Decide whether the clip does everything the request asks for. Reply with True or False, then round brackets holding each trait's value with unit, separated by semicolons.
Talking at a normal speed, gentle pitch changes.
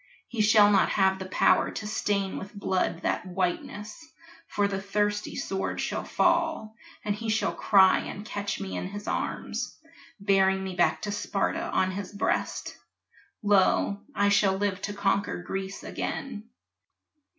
True (150 wpm; 1.4 semitones)